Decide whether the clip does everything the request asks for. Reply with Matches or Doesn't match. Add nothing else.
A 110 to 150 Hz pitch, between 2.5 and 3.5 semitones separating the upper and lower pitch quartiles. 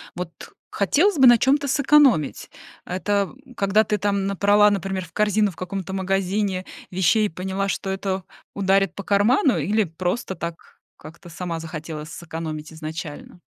Doesn't match